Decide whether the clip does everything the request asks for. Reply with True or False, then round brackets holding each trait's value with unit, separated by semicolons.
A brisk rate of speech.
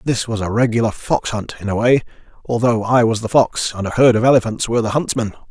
True (240 wpm)